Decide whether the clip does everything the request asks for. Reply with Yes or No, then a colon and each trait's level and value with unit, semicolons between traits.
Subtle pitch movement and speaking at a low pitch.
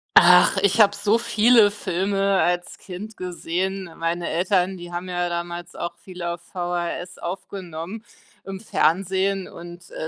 No: narrow, 2.1 semitones; medium, 180 Hz